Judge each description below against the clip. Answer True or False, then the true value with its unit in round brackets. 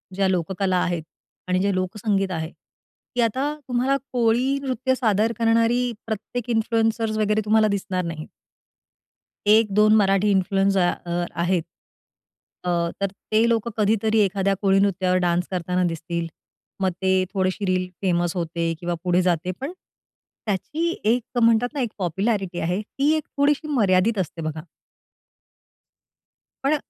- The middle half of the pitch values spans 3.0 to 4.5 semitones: True (3.9 semitones)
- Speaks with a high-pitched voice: True (200 Hz)